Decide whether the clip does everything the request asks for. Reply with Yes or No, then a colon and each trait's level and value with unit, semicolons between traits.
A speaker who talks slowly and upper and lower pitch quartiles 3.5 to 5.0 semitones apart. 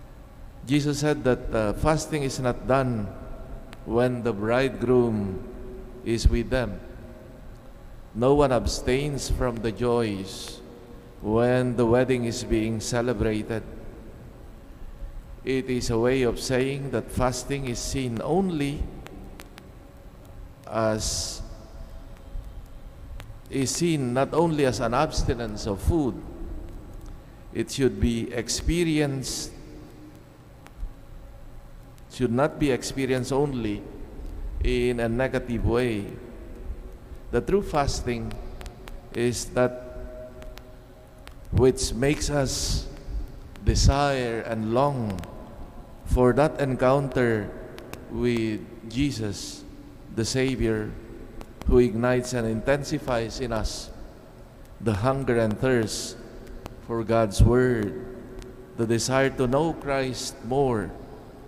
No: slow, 95 wpm; average, 2.7 semitones